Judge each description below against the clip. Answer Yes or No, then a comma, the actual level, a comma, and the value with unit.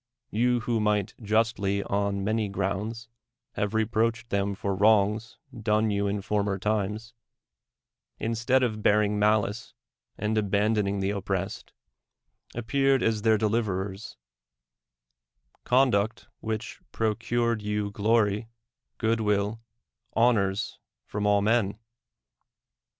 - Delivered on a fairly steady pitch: Yes, narrow, 1.9 semitones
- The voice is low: Yes, low, 105 Hz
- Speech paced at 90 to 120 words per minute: Yes, slow, 110 wpm